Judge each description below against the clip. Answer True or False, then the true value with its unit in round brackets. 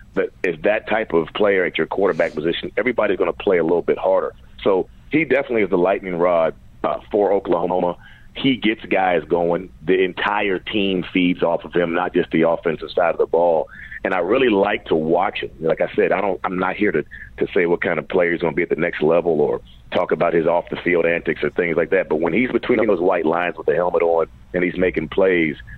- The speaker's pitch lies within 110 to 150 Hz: True (135 Hz)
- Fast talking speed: True (235 wpm)